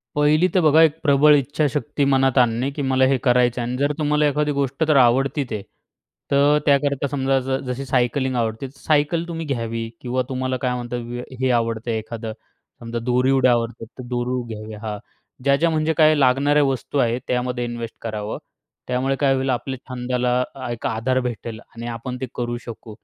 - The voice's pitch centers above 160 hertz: No, low, 130 Hz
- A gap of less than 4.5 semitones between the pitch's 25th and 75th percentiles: Yes, average, 2.9 semitones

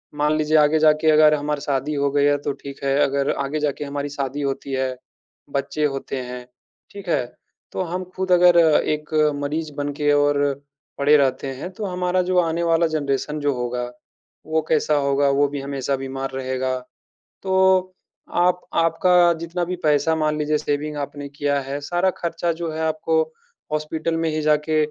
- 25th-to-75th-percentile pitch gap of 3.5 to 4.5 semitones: No, average, 2.7 semitones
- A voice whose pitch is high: No, medium, 150 Hz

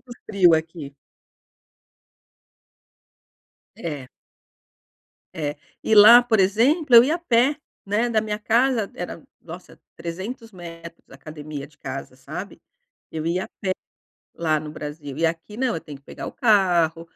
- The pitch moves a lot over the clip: Yes, wide, 6.4 semitones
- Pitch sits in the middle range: Yes, medium, 180 Hz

